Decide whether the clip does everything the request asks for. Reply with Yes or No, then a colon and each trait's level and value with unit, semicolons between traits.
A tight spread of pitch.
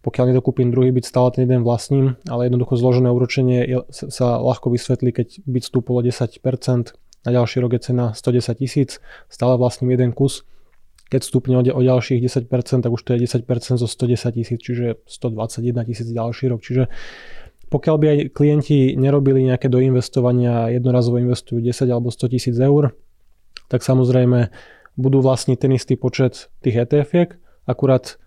Yes: narrow, 1.1 semitones